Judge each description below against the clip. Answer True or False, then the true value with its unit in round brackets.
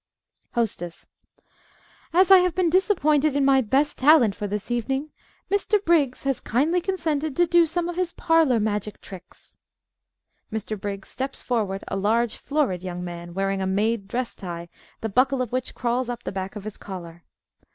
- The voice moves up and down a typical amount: False (7.6 semitones)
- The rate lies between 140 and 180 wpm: True (175 wpm)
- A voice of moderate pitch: False (245 Hz)